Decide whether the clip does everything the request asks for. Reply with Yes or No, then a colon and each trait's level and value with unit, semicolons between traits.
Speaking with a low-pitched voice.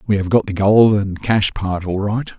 Yes: low, 100 Hz